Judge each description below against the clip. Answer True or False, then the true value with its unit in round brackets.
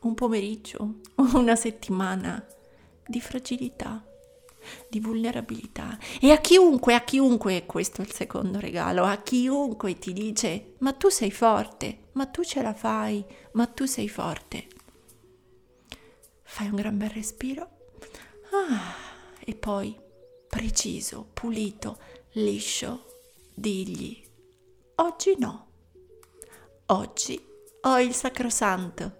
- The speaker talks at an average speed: False (110 wpm)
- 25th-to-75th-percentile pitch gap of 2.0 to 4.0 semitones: False (5.1 semitones)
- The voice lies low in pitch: False (230 Hz)